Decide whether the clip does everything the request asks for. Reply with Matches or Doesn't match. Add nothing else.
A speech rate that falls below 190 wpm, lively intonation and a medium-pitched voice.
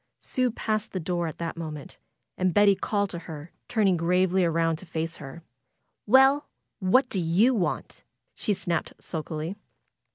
Doesn't match